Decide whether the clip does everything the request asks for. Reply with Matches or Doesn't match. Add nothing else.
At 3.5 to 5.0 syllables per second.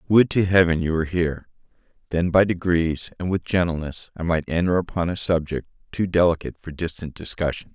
Doesn't match